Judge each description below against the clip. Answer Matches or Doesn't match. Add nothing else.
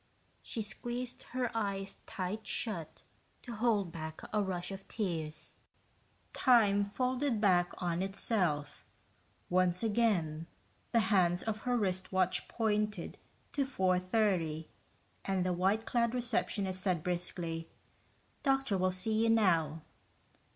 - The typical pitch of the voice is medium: Doesn't match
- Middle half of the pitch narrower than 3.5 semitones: Doesn't match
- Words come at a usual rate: Doesn't match